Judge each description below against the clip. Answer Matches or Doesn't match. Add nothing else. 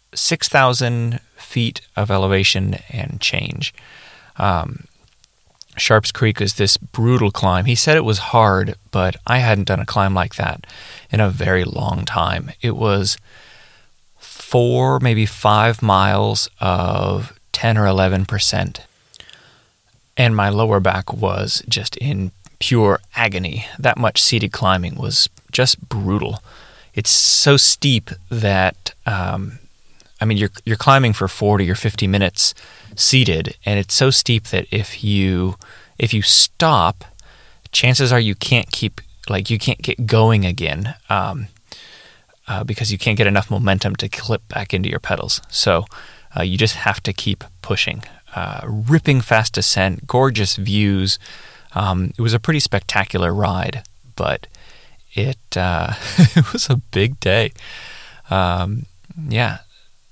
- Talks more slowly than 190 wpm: Matches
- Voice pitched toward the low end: Matches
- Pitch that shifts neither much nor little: Matches